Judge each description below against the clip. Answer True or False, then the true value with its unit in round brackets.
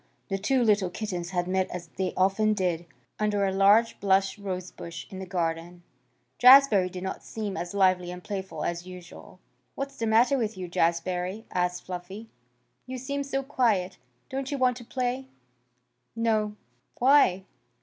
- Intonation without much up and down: False (4.2 semitones)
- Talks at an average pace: True (160 wpm)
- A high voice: True (195 Hz)